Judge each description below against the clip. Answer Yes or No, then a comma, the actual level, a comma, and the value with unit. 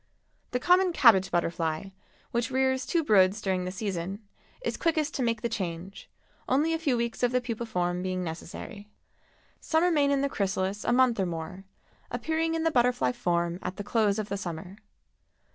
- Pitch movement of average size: No, wide, 6.2 semitones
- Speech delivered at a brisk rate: No, average, 180 wpm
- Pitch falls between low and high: No, high, 210 Hz